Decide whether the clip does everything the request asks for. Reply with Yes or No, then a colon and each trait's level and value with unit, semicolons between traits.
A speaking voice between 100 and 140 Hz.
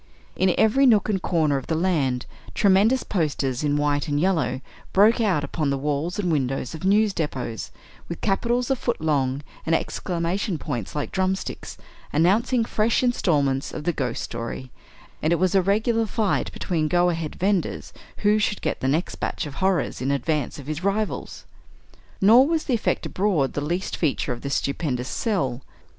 No: medium, 170 Hz